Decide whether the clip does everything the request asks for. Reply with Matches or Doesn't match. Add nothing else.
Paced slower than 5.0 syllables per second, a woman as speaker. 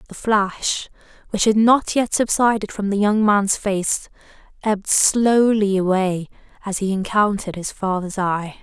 Matches